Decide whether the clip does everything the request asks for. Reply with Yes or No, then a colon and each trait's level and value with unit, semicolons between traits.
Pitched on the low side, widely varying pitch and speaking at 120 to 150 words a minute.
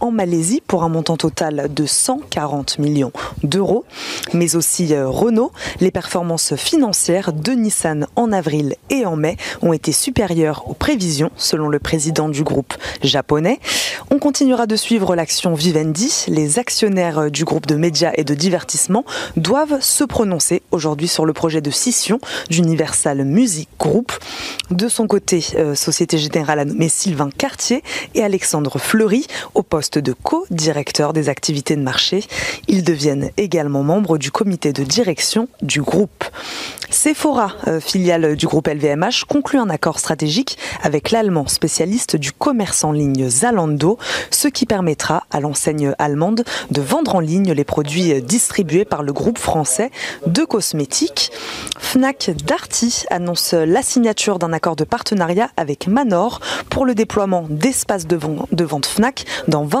No: medium, 170 Hz; wide, 6.5 semitones; slow, 145 wpm